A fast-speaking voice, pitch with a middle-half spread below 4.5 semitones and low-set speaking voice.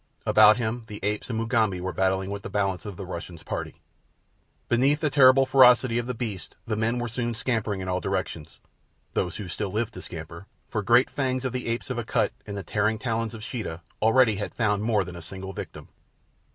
Yes: fast, 210 wpm; average, 3.7 semitones; low, 110 Hz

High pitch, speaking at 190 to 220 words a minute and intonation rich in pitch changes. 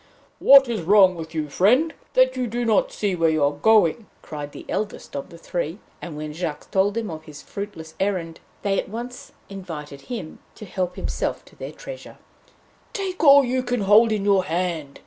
Yes: high, 195 Hz; average, 195 wpm; wide, 6.1 semitones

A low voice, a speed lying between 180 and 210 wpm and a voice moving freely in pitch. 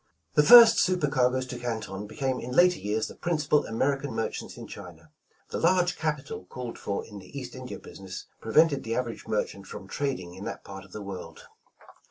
Yes: low, 125 Hz; average, 190 wpm; wide, 6.3 semitones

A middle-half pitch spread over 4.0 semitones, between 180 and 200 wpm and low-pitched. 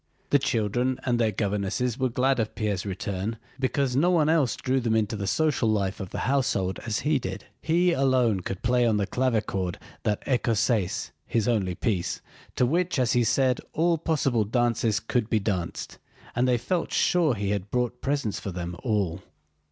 Yes: average, 4.4 semitones; average, 185 wpm; low, 115 Hz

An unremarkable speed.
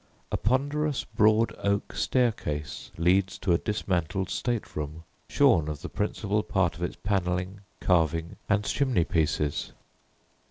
No: slow, 130 wpm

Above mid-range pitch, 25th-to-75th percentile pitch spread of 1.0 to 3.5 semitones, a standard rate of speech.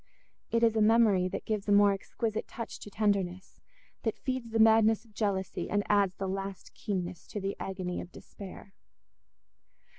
Yes: high, 205 Hz; narrow, 2.4 semitones; average, 170 wpm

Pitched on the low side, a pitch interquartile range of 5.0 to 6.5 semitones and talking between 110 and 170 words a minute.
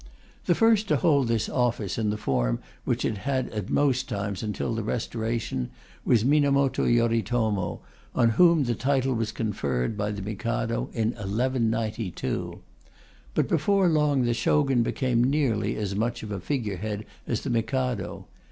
No: low, 115 Hz; average, 3.9 semitones; average, 155 wpm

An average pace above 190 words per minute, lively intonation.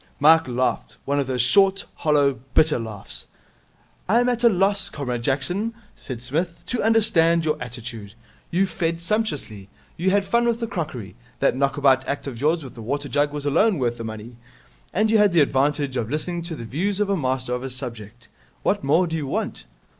Yes: average, 200 wpm; wide, 6.8 semitones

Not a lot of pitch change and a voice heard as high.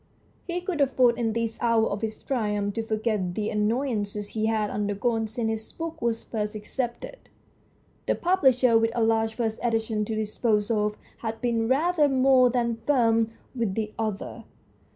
Yes: narrow, 2.3 semitones; high, 225 Hz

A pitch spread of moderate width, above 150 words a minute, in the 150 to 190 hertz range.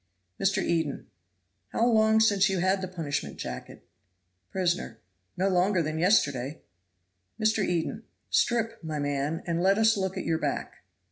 No: average, 4.2 semitones; average, 145 wpm; medium, 185 Hz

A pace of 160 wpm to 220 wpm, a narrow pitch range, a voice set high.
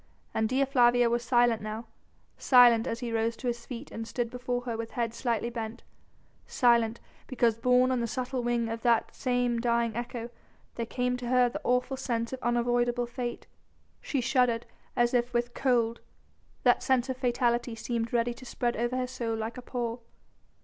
Yes: average, 185 wpm; narrow, 1.2 semitones; high, 240 Hz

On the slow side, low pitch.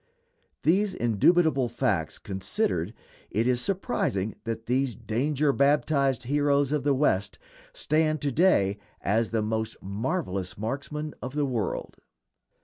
Yes: slow, 125 wpm; low, 130 Hz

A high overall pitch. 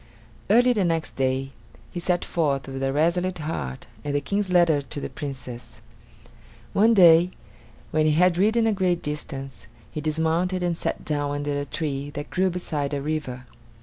No: medium, 155 Hz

